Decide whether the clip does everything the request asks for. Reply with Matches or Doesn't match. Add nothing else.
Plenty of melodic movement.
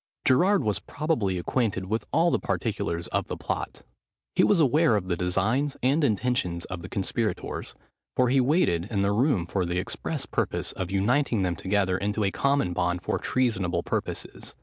Matches